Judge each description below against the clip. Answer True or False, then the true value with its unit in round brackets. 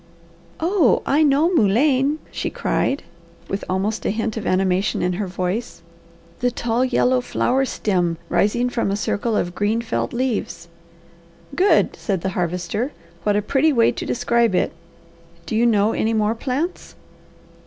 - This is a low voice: False (225 Hz)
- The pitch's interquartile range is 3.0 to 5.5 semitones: True (4.6 semitones)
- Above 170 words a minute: False (155 wpm)